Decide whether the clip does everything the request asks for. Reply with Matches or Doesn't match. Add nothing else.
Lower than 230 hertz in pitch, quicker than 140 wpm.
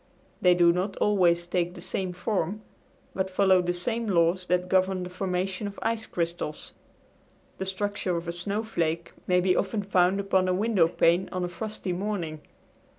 Matches